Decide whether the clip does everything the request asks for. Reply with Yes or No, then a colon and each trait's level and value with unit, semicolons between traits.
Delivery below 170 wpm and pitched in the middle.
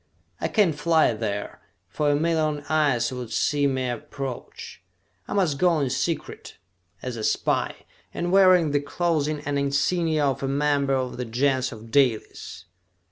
Yes: average, 155 wpm; medium, 145 Hz